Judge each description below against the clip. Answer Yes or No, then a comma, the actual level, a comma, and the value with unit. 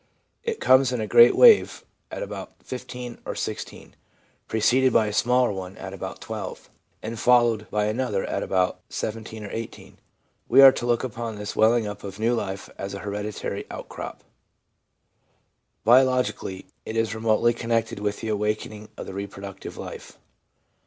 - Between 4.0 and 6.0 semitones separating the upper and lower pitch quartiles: No, average, 2.8 semitones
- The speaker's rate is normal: Yes, average, 160 wpm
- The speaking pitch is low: Yes, low, 110 Hz